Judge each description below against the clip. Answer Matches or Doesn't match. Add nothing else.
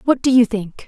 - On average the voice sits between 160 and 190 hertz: Doesn't match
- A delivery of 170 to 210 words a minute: Doesn't match